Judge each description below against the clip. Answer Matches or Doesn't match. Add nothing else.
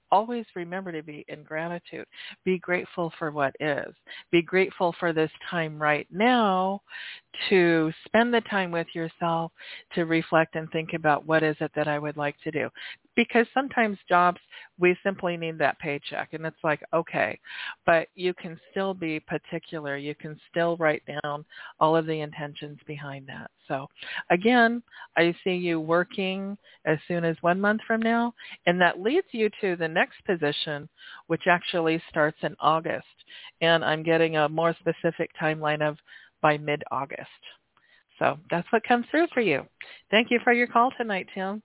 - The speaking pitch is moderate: Matches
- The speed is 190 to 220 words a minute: Doesn't match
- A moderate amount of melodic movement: Matches